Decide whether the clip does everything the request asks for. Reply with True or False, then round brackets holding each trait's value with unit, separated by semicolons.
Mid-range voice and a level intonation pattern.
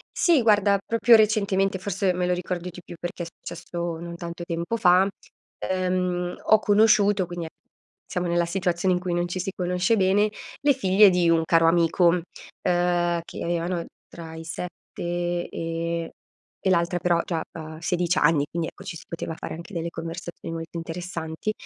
True (175 Hz; 1.9 semitones)